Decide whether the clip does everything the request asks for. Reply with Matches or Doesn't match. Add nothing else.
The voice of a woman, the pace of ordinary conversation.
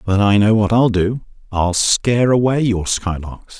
Doesn't match